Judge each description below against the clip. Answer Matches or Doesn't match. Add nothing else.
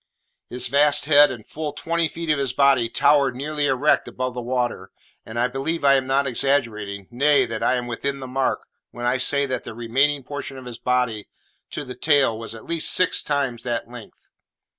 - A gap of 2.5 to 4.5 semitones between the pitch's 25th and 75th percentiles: Matches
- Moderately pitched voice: Doesn't match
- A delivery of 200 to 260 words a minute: Matches